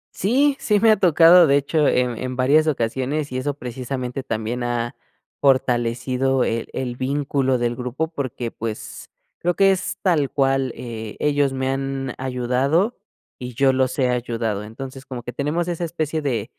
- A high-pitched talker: No, low, 130 Hz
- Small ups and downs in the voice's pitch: No, average, 3.2 semitones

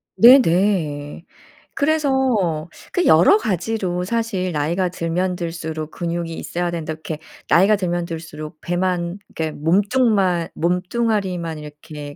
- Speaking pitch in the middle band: Yes, medium, 175 Hz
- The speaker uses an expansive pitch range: No, average, 3.3 semitones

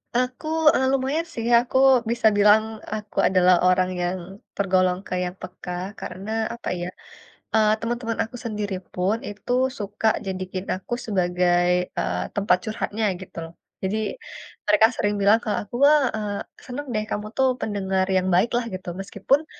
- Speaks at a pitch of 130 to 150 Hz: No, high, 205 Hz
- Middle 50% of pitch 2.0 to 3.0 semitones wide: No, average, 3.5 semitones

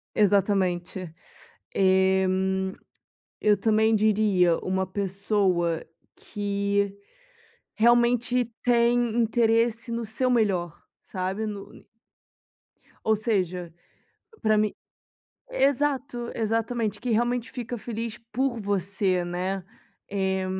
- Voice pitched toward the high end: Yes, high, 210 Hz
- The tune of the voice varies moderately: Yes, average, 3.6 semitones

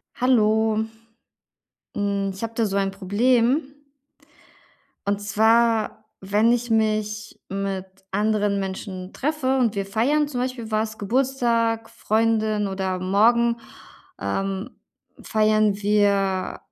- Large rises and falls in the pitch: No, average, 2.7 semitones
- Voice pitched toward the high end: Yes, high, 215 Hz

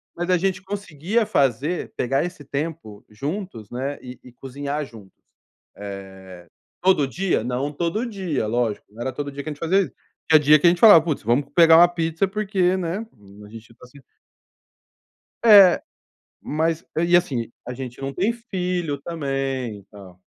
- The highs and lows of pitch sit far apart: Yes, wide, 6.1 semitones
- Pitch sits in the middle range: Yes, medium, 150 Hz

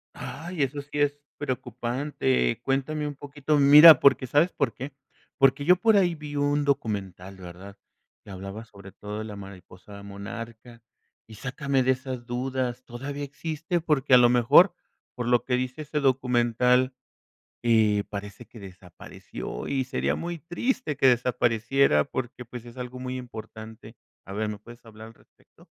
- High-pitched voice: No, low, 125 Hz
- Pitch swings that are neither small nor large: Yes, average, 4.6 semitones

